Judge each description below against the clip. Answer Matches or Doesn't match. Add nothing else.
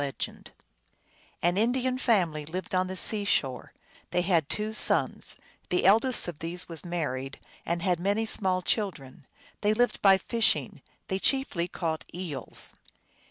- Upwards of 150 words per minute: Doesn't match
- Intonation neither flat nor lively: Matches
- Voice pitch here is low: Doesn't match